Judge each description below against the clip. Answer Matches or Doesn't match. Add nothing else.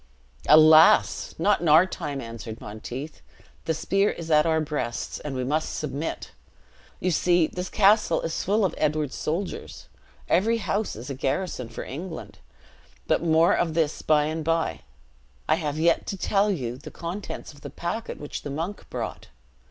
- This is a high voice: Doesn't match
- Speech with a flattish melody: Doesn't match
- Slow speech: Doesn't match